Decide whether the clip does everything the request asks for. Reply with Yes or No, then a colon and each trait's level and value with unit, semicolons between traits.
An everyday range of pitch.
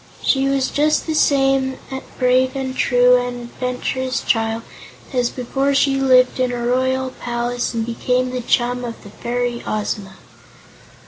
No: narrow, 1.5 semitones